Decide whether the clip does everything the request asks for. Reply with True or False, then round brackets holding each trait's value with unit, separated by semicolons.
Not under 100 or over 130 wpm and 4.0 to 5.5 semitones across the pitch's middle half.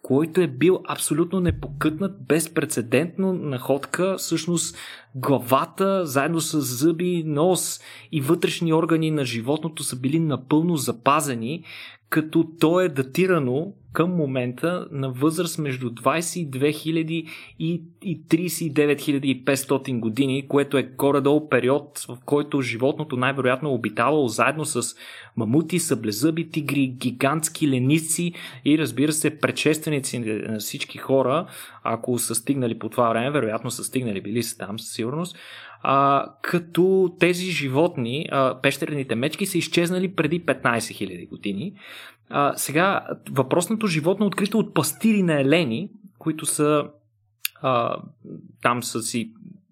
True (125 wpm; 4.3 semitones)